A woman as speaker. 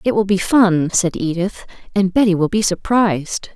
Yes: female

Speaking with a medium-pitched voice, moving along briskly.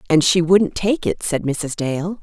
Yes: medium, 170 Hz; fast, 215 wpm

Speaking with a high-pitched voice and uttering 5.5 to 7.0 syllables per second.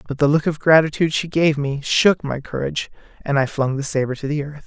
No: medium, 150 Hz; 5.9 syllables/s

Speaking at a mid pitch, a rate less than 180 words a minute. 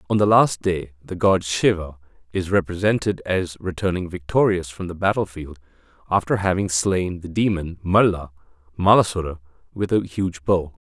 No: very low, 90 Hz; average, 145 wpm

